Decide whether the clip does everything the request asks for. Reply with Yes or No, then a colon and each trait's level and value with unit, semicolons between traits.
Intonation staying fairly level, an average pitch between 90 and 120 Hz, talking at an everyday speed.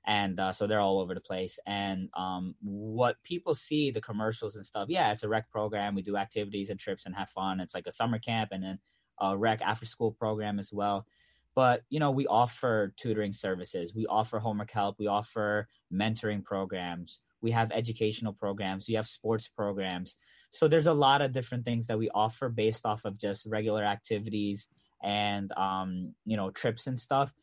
Yes: narrow, 2.2 semitones; low, 105 Hz; average, 195 wpm